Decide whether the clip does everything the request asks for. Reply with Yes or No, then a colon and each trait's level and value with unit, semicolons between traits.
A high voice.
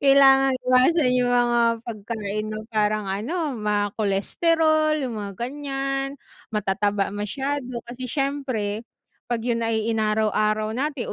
Yes: high, 235 Hz